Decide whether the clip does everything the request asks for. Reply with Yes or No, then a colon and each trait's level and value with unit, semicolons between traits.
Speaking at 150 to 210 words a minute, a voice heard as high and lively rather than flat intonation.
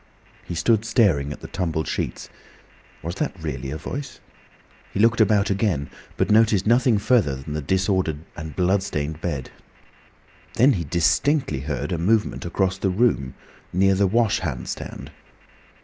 No: average, 155 wpm; very low, 95 Hz; wide, 5.7 semitones